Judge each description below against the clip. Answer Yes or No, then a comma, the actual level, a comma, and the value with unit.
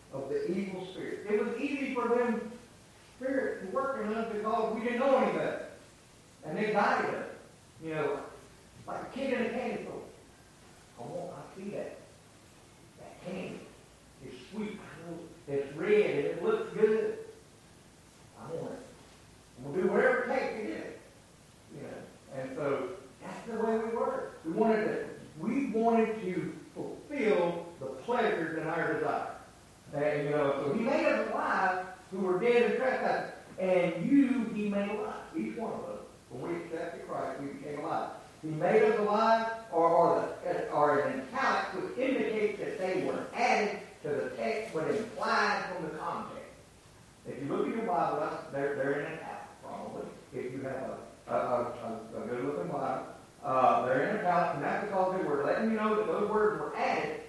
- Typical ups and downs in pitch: No, wide, 6.2 semitones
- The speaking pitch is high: Yes, high, 210 Hz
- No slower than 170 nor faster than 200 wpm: Yes, average, 175 wpm